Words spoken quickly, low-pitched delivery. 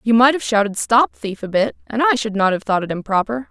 No: fast, 275 wpm; high, 225 Hz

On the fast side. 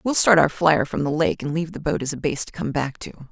Yes: fast, 325 wpm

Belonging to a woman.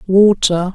Yes: female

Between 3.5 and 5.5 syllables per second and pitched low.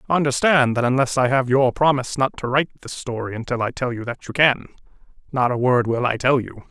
No: 6.1 syllables/s; low, 130 Hz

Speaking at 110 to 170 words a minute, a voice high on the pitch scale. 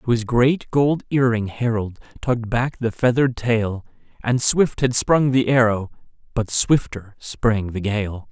No: average, 165 wpm; low, 120 Hz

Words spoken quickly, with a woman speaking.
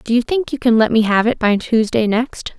Yes: fast, 280 wpm; female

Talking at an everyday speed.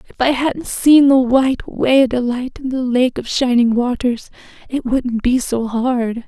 Yes: average, 190 wpm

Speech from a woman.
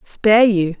Yes: female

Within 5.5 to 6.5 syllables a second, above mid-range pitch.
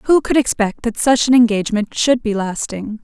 No: 5.0 syllables/s; high, 230 Hz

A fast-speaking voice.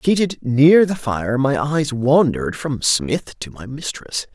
No: average, 165 wpm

